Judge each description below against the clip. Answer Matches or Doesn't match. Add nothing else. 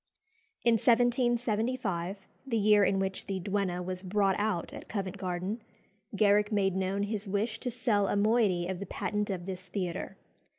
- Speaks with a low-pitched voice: Doesn't match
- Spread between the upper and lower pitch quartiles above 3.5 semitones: Doesn't match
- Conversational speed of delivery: Matches